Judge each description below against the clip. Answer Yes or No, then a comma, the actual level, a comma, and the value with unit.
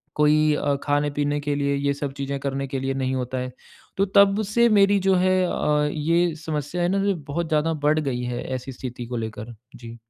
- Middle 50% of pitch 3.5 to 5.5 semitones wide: Yes, average, 4.0 semitones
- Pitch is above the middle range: No, medium, 145 Hz